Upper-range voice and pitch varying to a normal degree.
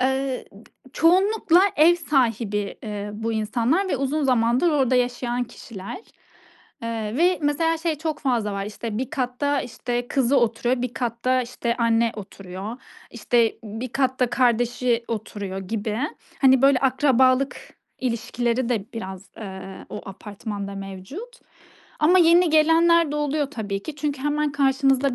Yes: very high, 250 Hz; average, 4.3 semitones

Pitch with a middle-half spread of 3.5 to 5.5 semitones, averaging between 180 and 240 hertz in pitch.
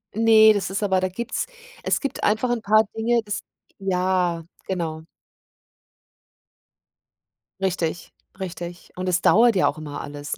Yes: average, 3.8 semitones; high, 190 Hz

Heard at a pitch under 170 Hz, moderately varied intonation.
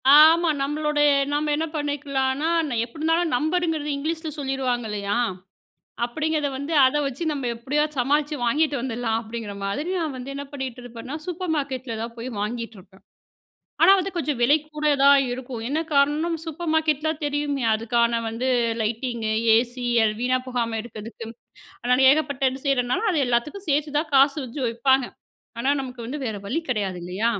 No: very high, 270 Hz; average, 4.1 semitones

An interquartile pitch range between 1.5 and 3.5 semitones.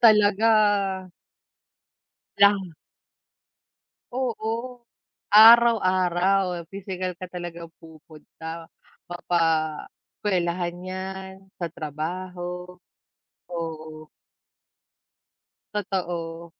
Yes: average, 2.9 semitones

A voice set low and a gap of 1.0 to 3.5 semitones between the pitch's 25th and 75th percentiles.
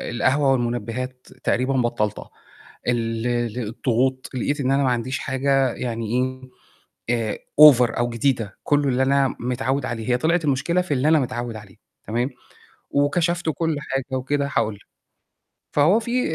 Yes: low, 130 Hz; average, 3.1 semitones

